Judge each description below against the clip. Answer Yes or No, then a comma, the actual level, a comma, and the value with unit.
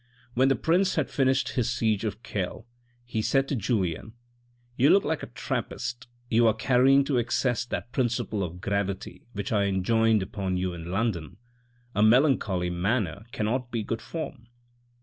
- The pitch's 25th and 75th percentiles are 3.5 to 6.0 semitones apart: Yes, average, 4.0 semitones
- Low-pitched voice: Yes, low, 115 Hz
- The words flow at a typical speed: Yes, average, 170 wpm